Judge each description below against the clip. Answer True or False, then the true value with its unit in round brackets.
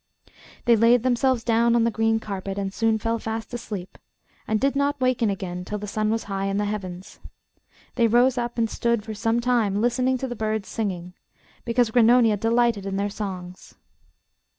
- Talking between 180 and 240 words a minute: True (185 wpm)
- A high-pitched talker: True (225 Hz)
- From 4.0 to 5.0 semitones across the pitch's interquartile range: False (2.9 semitones)